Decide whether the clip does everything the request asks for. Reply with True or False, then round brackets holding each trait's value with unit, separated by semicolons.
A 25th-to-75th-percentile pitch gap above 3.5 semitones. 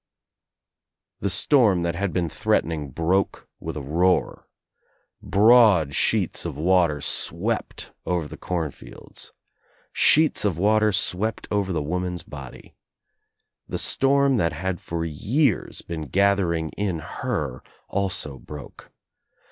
True (4.1 semitones)